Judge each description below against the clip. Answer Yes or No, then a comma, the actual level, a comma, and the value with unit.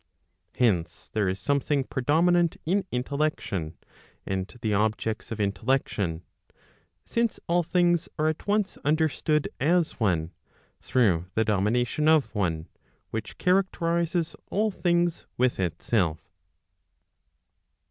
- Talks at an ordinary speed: No, slow, 105 wpm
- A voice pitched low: Yes, low, 130 Hz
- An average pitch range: No, wide, 9.0 semitones